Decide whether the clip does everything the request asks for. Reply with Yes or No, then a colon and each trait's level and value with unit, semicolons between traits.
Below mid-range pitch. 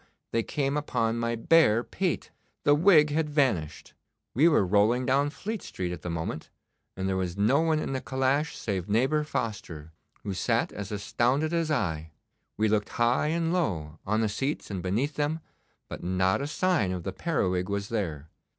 Yes: low, 115 Hz